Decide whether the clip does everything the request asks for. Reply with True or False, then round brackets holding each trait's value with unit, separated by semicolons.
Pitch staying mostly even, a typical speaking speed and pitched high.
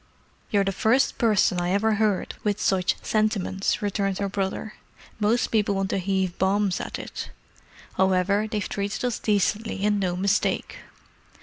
True (1.9 semitones; 150 wpm; 200 Hz)